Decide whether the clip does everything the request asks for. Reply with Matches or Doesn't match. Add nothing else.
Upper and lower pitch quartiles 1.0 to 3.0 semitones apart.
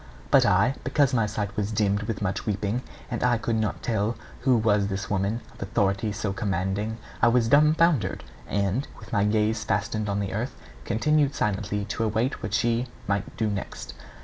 Matches